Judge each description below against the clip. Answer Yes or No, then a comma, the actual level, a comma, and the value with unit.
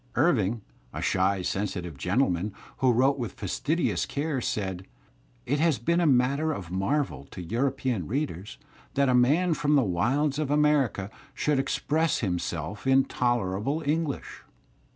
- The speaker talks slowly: No, average, 150 wpm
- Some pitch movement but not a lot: No, wide, 7.1 semitones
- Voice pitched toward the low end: Yes, low, 130 Hz